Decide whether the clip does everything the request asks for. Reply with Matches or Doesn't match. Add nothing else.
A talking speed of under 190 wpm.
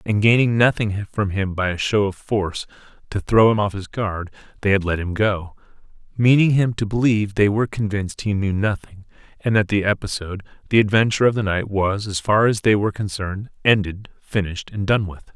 Doesn't match